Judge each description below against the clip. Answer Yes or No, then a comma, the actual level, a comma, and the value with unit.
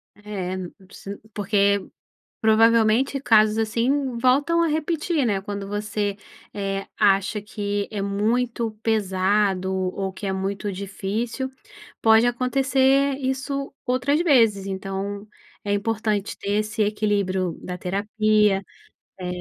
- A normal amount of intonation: Yes, average, 3.5 semitones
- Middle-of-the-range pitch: No, high, 210 Hz